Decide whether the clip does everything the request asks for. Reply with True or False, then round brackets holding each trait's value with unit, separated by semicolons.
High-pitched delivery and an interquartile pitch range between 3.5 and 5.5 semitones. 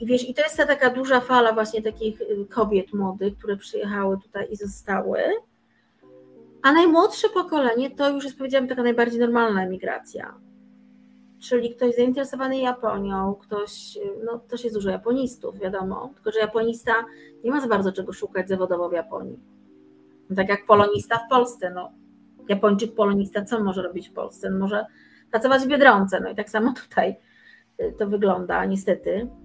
True (220 Hz; 4.1 semitones)